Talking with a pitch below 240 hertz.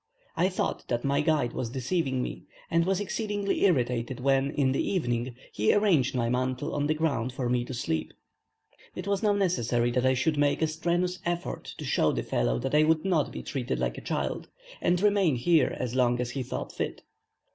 Yes: medium, 140 Hz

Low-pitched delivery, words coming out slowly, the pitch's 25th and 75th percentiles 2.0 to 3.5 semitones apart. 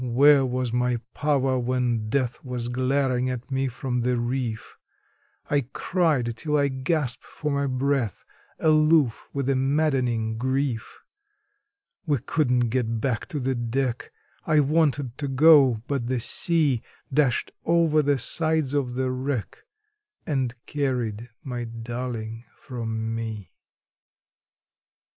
Yes: low, 130 Hz; slow, 125 wpm; average, 2.9 semitones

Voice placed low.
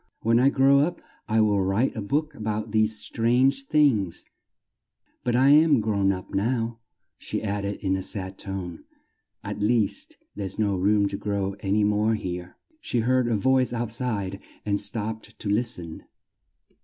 Yes: low, 110 Hz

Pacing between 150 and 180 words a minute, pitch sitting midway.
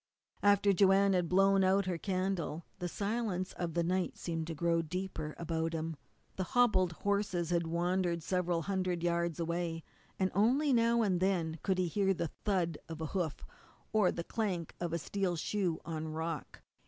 Yes: average, 175 wpm; medium, 180 Hz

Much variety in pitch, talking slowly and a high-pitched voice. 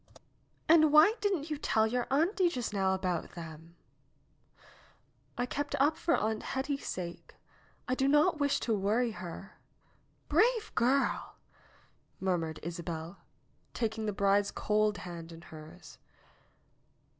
Yes: wide, 8.2 semitones; slow, 130 wpm; high, 220 Hz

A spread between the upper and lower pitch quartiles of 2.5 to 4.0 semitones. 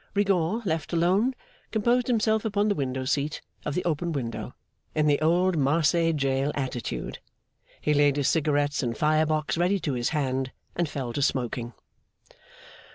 No: average, 4.4 semitones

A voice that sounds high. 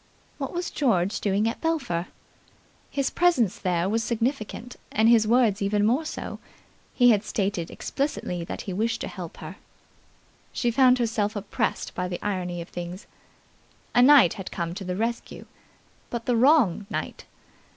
Yes: high, 220 Hz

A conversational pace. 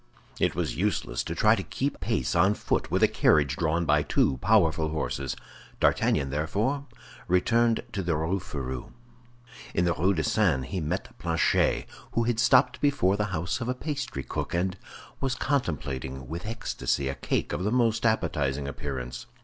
Yes: average, 170 wpm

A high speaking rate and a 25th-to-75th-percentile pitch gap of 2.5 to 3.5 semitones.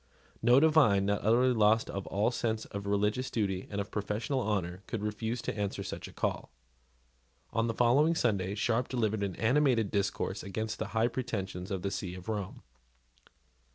No: average, 175 wpm; average, 2.9 semitones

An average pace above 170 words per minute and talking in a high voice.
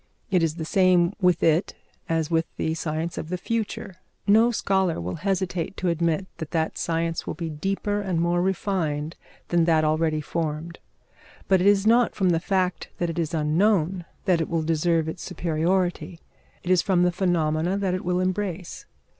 No: average, 180 wpm; medium, 175 Hz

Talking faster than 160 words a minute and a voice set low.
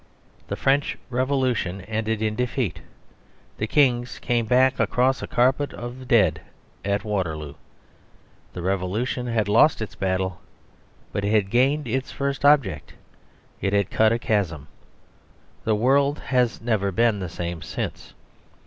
No: average, 140 wpm; low, 110 Hz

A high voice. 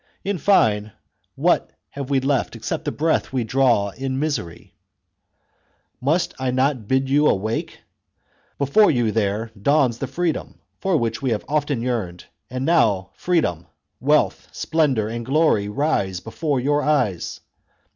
No: low, 130 Hz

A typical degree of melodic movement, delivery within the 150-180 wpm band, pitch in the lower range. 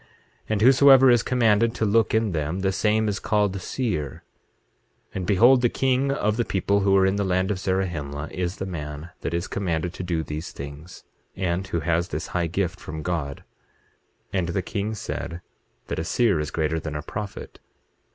No: average, 4.5 semitones; average, 195 wpm; very low, 95 Hz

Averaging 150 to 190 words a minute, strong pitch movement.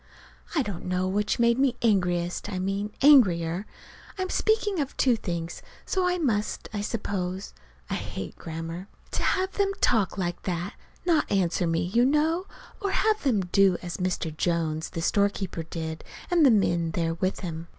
Yes: average, 170 wpm; wide, 6.8 semitones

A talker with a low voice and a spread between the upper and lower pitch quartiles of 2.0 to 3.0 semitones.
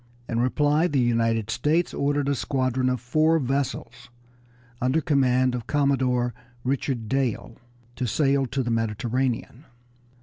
Yes: low, 130 Hz; average, 2.7 semitones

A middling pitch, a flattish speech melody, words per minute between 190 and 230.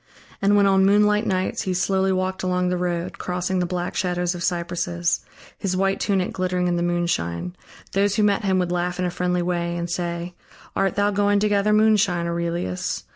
Yes: medium, 180 Hz; narrow, 2.0 semitones; average, 195 wpm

